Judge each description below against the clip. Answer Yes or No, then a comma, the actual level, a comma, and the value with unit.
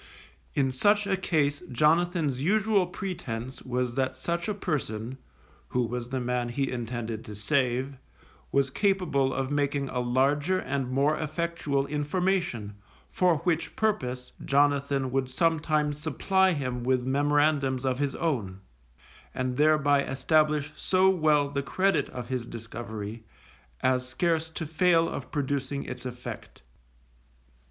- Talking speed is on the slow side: Yes, slow, 130 wpm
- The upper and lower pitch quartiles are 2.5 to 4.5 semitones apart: Yes, average, 4.1 semitones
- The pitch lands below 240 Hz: Yes, medium, 140 Hz